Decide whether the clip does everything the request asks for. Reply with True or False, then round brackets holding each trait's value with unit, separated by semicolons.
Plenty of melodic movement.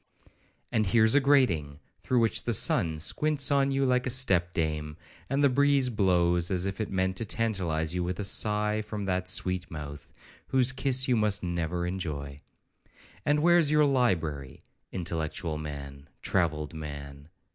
True (8.0 semitones)